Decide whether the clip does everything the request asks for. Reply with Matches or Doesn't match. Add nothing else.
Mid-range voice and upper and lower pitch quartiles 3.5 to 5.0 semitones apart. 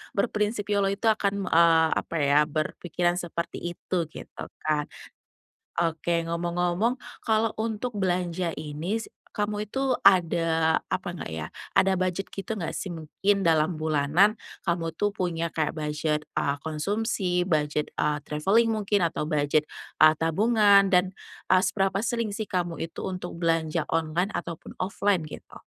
Matches